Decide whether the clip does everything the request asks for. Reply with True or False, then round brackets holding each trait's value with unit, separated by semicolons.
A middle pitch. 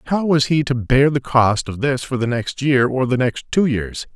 False (130 Hz)